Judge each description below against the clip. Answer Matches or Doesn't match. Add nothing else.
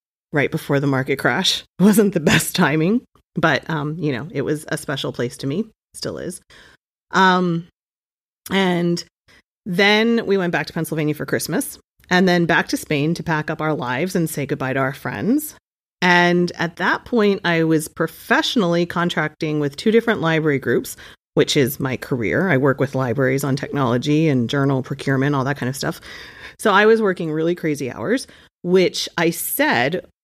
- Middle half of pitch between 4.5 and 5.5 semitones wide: Doesn't match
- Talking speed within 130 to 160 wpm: Doesn't match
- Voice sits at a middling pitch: Matches